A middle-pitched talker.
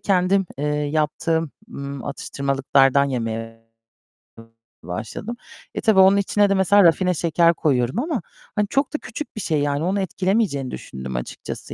Yes: medium, 160 Hz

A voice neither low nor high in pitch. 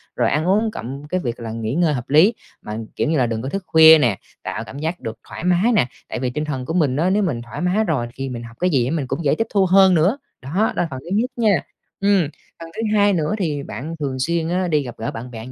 Yes: medium, 155 Hz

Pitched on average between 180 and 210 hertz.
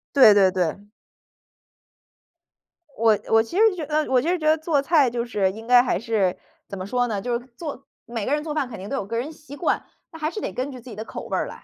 No: high, 245 Hz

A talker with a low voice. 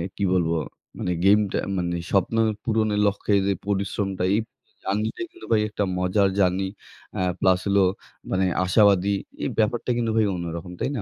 Yes: low, 100 Hz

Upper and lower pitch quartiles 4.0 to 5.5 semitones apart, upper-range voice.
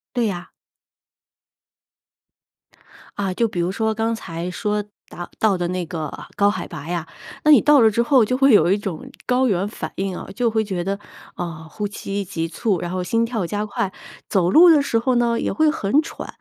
Yes: average, 4.7 semitones; high, 205 Hz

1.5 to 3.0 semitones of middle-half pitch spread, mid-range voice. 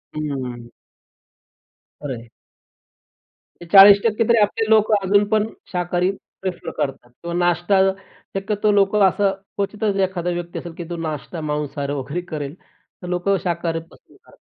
No: average, 4.1 semitones; medium, 180 Hz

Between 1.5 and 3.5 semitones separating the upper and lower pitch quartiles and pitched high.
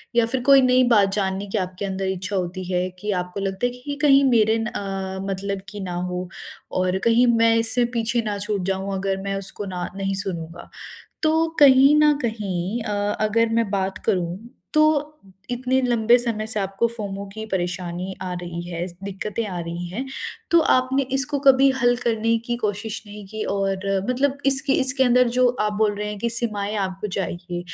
No: average, 3.9 semitones; high, 210 Hz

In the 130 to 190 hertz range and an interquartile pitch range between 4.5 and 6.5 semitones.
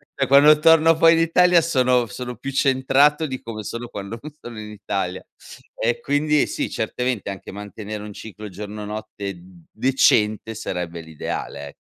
No: low, 115 Hz; average, 5.2 semitones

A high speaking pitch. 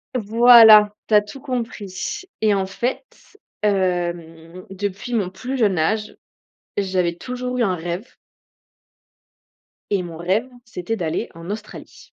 Yes: high, 200 Hz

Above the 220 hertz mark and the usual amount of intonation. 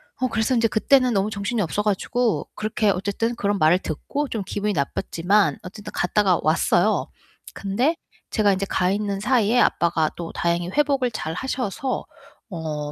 No: high, 205 Hz; average, 4.5 semitones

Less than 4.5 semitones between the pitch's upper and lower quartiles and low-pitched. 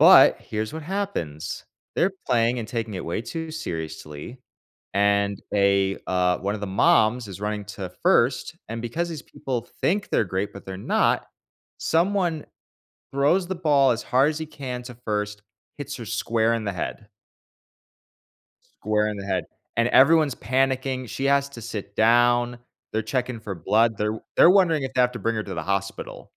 No: average, 5.0 semitones; low, 115 Hz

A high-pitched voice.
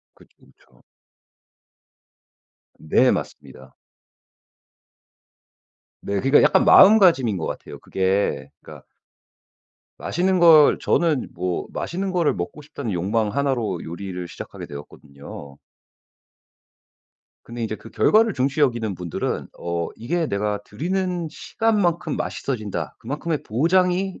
No: low, 130 Hz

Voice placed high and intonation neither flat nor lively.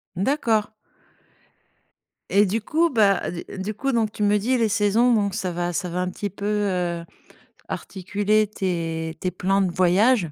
Yes: high, 200 Hz; average, 3.0 semitones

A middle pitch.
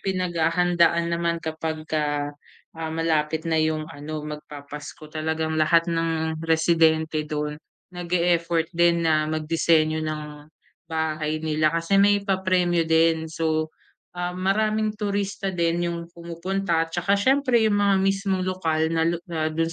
Yes: medium, 165 Hz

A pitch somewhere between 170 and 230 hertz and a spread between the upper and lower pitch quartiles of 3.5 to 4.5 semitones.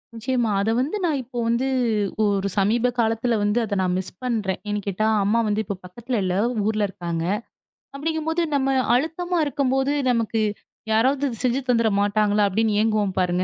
Yes: high, 225 Hz; average, 4.1 semitones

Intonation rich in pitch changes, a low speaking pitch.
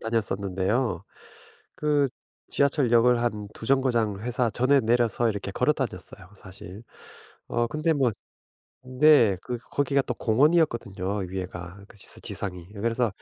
No: average, 4.8 semitones; low, 115 Hz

